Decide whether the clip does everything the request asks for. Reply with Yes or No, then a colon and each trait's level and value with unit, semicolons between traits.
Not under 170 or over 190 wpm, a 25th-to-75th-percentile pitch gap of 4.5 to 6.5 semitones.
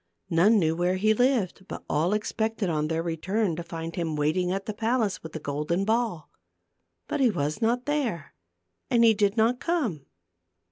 Yes: average, 180 wpm; wide, 5.5 semitones